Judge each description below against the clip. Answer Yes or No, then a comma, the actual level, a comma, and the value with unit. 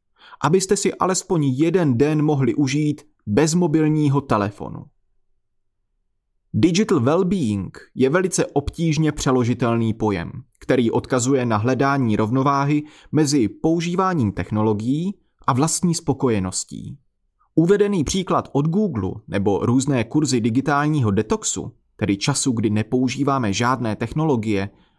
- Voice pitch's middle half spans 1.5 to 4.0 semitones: No, wide, 6.3 semitones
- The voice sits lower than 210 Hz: Yes, low, 135 Hz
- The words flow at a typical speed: No, slow, 105 wpm